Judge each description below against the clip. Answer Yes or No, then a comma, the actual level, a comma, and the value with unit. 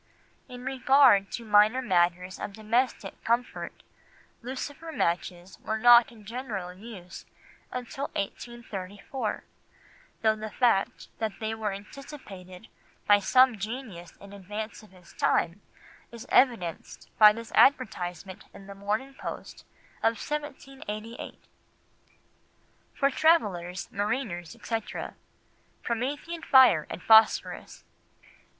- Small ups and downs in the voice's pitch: No, average, 4.5 semitones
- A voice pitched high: Yes, high, 220 Hz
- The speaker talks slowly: Yes, slow, 105 wpm